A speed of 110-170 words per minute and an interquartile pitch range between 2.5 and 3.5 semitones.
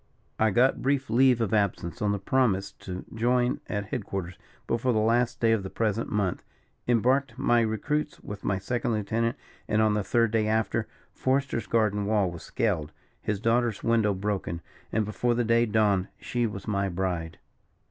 No: average, 180 wpm; average, 3.0 semitones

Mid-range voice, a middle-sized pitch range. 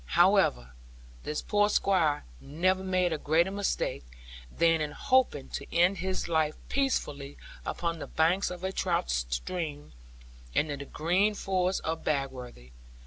Yes: medium, 165 Hz; average, 4.5 semitones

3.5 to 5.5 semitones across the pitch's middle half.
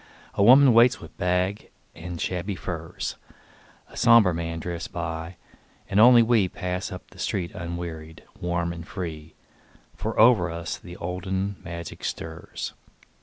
No: average, 3.1 semitones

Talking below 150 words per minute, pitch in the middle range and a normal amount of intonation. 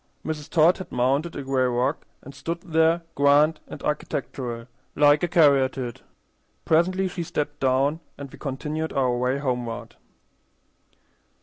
Yes: slow, 135 wpm; medium, 145 Hz; average, 3.6 semitones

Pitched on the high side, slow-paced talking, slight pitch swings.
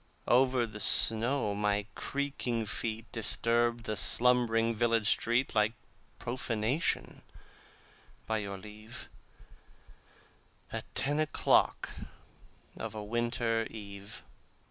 No: low, 115 Hz; slow, 95 wpm; narrow, 2.1 semitones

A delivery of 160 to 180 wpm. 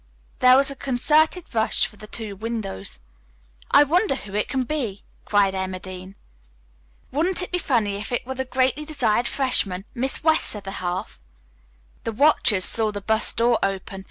Yes: average, 170 wpm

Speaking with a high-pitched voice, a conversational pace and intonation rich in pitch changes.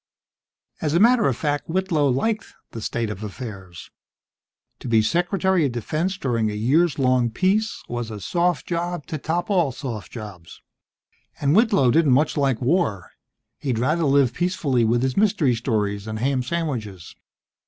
No: low, 135 Hz; average, 160 wpm; wide, 7.0 semitones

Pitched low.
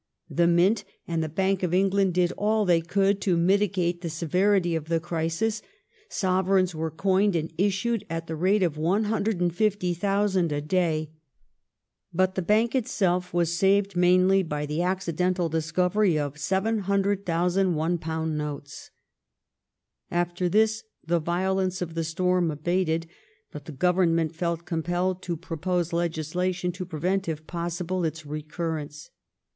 No: medium, 175 Hz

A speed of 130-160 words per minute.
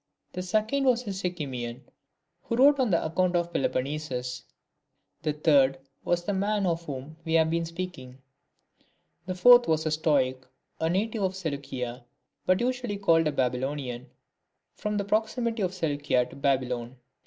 Yes: average, 155 wpm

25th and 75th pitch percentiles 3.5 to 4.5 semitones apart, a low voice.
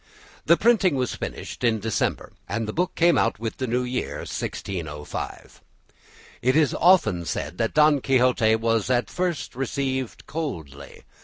No: average, 5.3 semitones; low, 125 Hz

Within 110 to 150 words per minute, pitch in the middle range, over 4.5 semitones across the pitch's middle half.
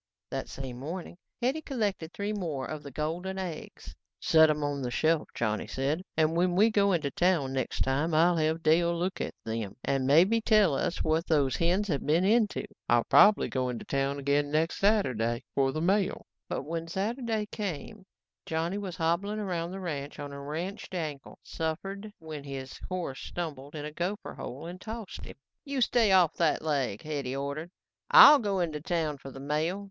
No: average, 185 wpm; medium, 160 Hz; average, 5.1 semitones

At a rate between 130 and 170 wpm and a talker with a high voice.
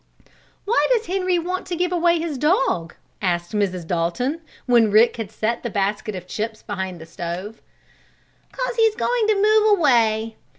Yes: average, 165 wpm; high, 235 Hz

